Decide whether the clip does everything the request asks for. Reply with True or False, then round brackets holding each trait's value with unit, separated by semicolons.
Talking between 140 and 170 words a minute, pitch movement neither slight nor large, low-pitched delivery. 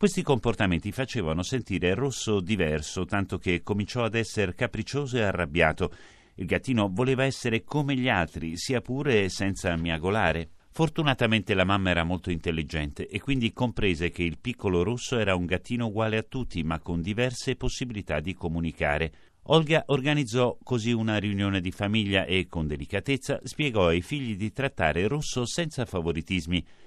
False (150 wpm; 6.1 semitones; 105 Hz)